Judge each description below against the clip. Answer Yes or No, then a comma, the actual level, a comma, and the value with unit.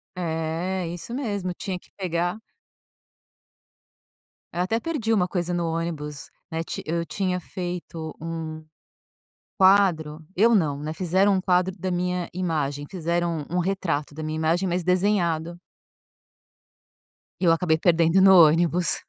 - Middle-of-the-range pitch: Yes, medium, 175 Hz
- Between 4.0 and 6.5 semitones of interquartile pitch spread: No, narrow, 2.4 semitones